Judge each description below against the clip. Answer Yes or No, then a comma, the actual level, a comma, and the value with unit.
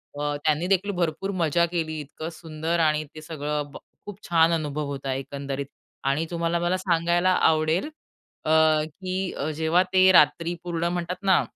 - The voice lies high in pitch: No, medium, 165 Hz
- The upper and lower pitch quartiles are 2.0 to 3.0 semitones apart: Yes, narrow, 2.5 semitones